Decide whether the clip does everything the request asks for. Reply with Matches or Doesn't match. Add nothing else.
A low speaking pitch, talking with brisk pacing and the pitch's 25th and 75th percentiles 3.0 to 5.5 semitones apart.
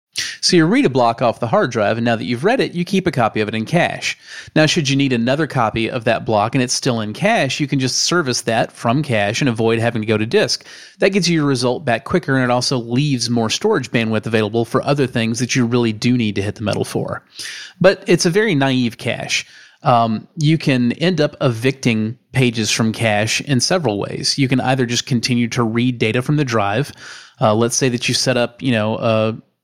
Matches